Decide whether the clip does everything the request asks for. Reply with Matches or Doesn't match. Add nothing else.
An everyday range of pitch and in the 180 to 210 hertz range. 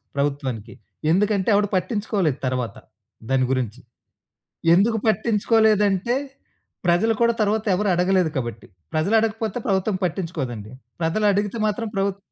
Doesn't match